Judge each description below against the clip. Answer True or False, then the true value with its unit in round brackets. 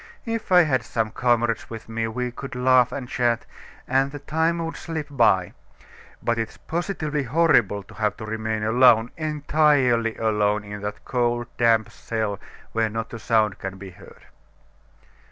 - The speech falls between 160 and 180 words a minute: True (165 wpm)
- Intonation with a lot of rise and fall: False (4.2 semitones)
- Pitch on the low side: True (120 Hz)